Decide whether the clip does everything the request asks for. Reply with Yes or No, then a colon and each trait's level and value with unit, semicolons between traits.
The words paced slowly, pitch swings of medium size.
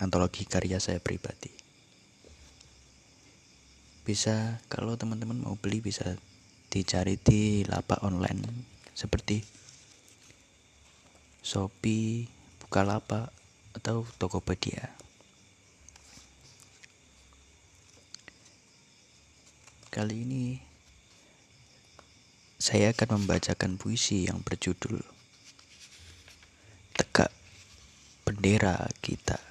Yes: slow, 60 wpm; average, 3.5 semitones